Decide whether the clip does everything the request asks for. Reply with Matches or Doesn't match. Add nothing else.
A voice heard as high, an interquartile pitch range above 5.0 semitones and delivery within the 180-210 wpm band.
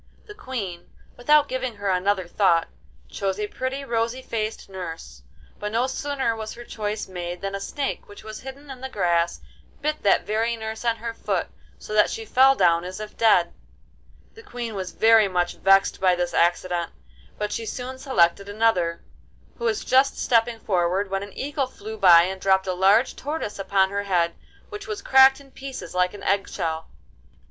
Matches